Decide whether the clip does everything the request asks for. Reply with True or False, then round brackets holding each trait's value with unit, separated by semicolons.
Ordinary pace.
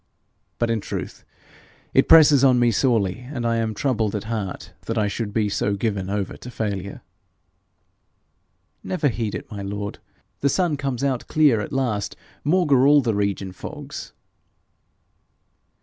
True (150 wpm)